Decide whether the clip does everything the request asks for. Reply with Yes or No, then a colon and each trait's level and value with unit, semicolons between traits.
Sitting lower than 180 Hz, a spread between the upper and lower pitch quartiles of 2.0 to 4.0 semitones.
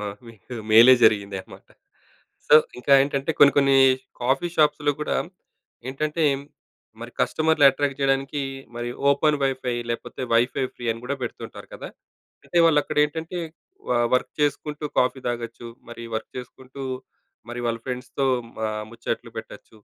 Yes: low, 135 Hz; average, 3.5 semitones